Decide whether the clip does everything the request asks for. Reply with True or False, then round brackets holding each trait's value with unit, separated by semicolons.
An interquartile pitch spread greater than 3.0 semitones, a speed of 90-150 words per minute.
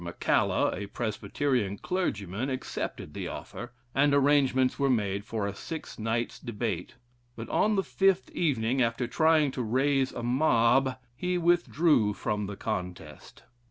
True (5.1 semitones; 140 wpm)